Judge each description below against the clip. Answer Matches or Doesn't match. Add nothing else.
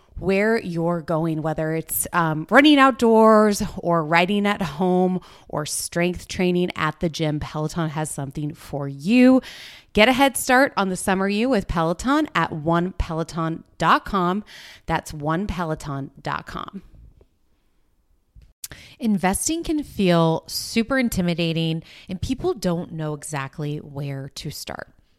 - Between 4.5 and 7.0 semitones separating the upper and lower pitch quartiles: Matches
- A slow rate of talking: Matches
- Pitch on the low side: Doesn't match